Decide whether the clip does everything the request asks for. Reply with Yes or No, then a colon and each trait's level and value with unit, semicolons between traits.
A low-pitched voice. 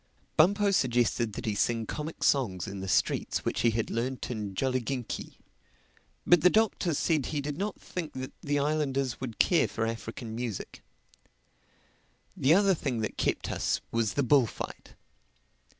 Yes: low, 130 Hz